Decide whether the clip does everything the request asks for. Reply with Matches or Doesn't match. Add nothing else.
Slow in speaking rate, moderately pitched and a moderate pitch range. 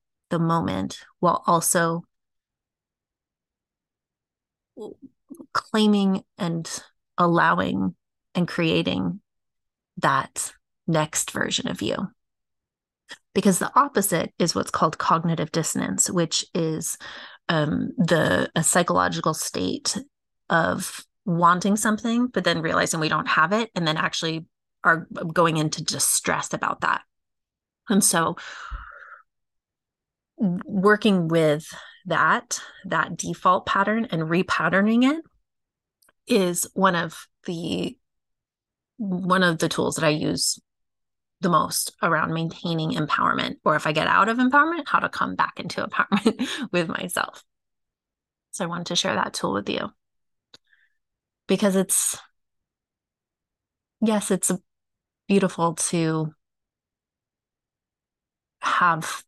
Matches